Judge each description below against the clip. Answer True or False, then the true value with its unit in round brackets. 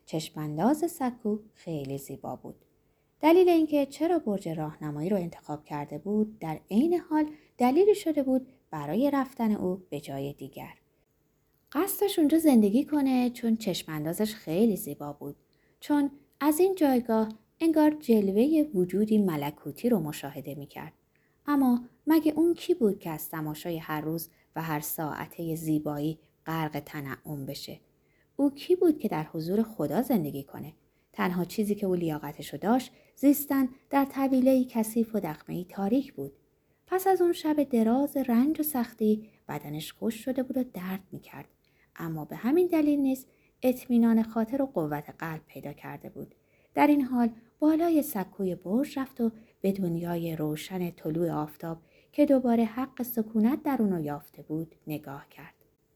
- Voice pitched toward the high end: True (215 Hz)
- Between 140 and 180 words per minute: True (150 wpm)